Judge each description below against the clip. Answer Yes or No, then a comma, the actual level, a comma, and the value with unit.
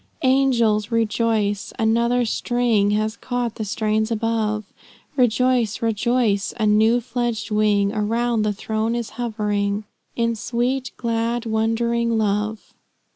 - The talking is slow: Yes, slow, 115 wpm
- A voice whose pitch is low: No, high, 225 Hz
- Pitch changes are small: Yes, narrow, 1.9 semitones